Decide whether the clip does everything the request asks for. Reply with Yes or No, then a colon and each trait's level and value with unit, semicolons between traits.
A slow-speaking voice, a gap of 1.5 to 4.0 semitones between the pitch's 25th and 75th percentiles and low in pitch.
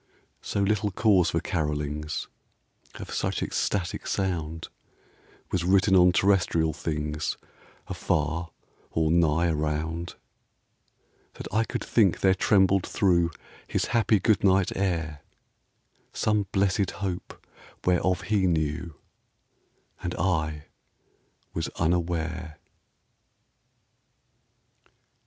Yes: slow, 95 wpm; average, 3.3 semitones; very low, 85 Hz